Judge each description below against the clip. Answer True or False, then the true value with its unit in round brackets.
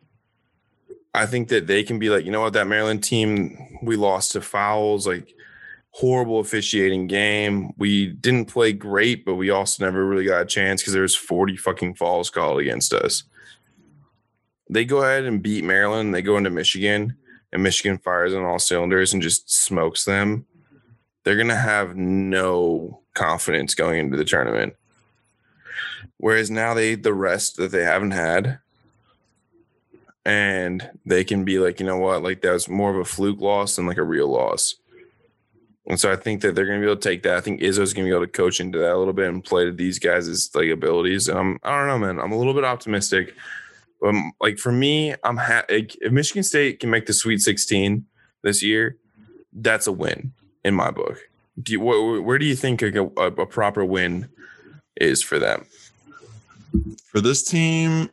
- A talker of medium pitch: False (105 Hz)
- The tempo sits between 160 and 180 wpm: False (195 wpm)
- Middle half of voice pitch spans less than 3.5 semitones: False (3.8 semitones)